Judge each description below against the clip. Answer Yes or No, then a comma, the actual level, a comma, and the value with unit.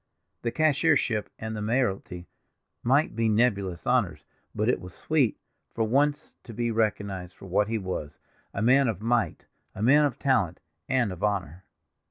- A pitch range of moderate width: Yes, average, 4.3 semitones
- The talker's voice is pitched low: Yes, low, 110 Hz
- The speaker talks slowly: No, average, 160 wpm